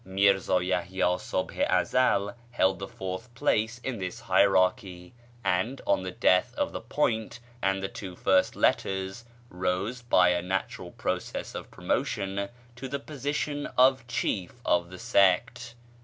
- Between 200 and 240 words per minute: No, average, 145 wpm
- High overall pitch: No, very low, 95 Hz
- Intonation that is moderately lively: Yes, average, 4.6 semitones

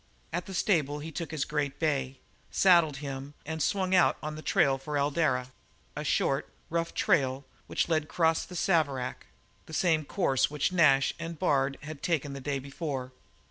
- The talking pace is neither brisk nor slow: Yes, average, 175 wpm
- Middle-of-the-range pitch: Yes, medium, 150 Hz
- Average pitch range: Yes, average, 3.3 semitones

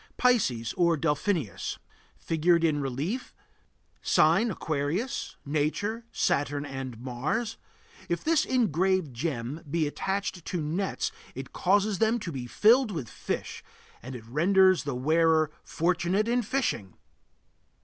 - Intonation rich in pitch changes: Yes, wide, 6.2 semitones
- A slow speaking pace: Yes, slow, 125 wpm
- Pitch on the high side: No, medium, 165 Hz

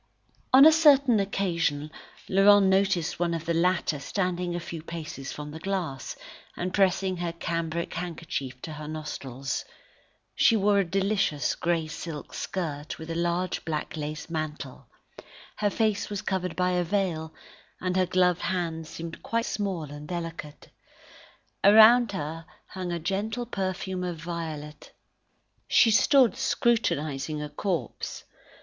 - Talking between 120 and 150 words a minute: Yes, average, 145 wpm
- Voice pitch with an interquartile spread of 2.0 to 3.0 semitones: No, average, 3.8 semitones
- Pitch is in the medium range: Yes, medium, 175 Hz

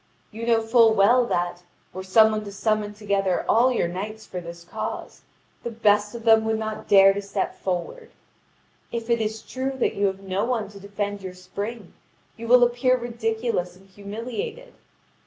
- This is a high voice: Yes, high, 215 Hz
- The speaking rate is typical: Yes, average, 180 wpm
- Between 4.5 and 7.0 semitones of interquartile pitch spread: No, average, 3.0 semitones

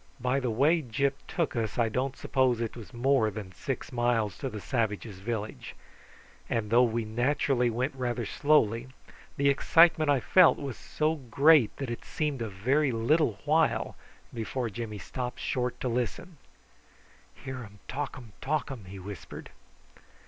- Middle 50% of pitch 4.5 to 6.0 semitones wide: No, average, 3.6 semitones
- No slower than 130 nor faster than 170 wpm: Yes, average, 155 wpm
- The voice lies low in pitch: Yes, low, 125 Hz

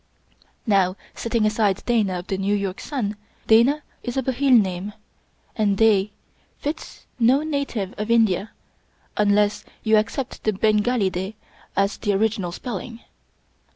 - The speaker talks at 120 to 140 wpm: Yes, slow, 135 wpm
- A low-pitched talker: No, high, 215 Hz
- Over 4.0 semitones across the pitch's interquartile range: No, average, 3.2 semitones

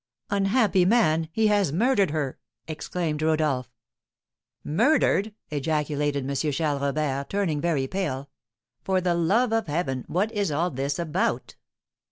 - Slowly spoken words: Yes, slow, 130 wpm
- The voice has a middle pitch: Yes, medium, 160 Hz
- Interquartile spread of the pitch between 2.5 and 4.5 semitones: No, average, 5.2 semitones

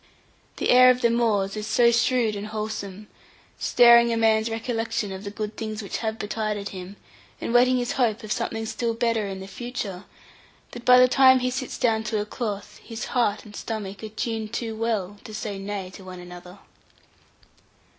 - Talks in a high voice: Yes, high, 220 Hz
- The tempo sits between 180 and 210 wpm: Yes, average, 190 wpm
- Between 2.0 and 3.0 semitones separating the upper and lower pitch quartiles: Yes, narrow, 2.5 semitones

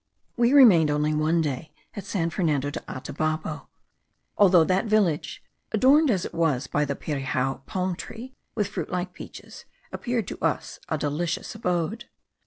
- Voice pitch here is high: No, medium, 170 Hz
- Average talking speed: Yes, average, 155 wpm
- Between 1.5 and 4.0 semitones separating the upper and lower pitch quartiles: No, wide, 5.6 semitones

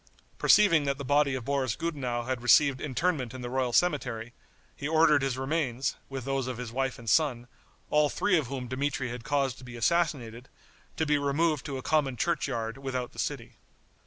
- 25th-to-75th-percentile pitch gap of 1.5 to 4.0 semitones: Yes, average, 3.1 semitones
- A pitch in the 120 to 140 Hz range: Yes, low, 135 Hz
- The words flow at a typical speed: Yes, average, 190 wpm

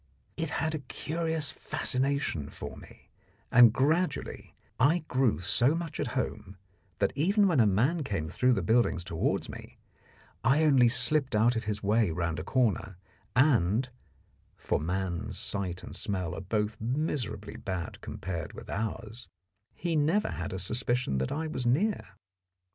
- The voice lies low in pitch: Yes, low, 120 Hz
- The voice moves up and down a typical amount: No, wide, 7.1 semitones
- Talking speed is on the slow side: No, average, 155 wpm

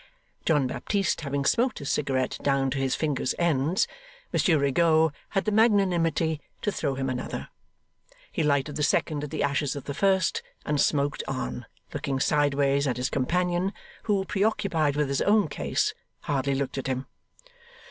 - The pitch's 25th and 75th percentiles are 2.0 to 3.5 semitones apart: No, average, 4.1 semitones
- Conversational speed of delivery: Yes, average, 160 wpm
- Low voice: No, medium, 145 Hz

